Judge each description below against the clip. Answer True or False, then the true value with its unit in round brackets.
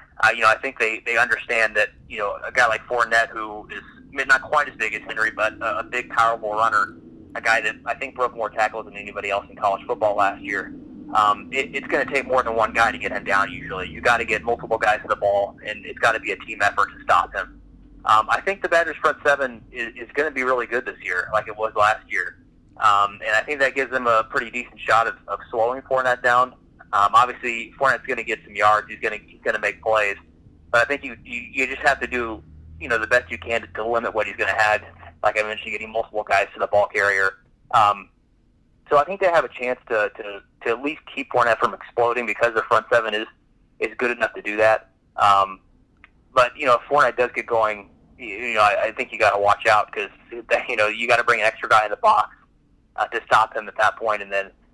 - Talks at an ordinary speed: False (260 wpm)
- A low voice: True (115 Hz)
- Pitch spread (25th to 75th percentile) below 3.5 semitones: True (3.0 semitones)